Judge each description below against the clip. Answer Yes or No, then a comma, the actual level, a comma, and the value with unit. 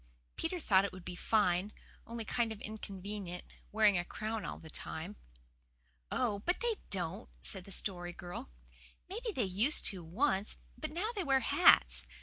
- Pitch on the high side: Yes, high, 205 Hz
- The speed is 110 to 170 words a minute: Yes, average, 165 wpm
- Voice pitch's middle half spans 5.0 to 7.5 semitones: Yes, wide, 5.4 semitones